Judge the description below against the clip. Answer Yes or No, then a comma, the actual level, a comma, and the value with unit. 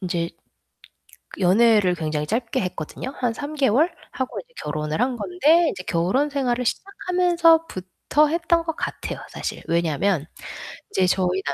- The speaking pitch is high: Yes, high, 235 Hz